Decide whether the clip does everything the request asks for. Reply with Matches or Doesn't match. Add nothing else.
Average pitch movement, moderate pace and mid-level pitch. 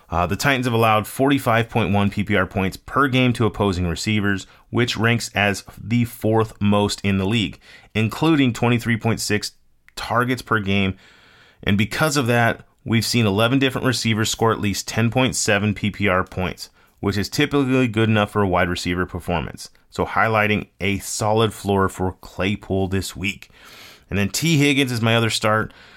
Doesn't match